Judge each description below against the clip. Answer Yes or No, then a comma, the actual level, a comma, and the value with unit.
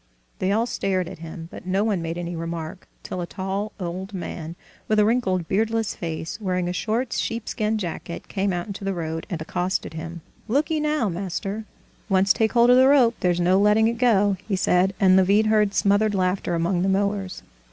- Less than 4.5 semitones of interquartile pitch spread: Yes, average, 3.4 semitones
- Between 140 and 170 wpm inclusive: No, average, 195 wpm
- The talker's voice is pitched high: Yes, high, 195 Hz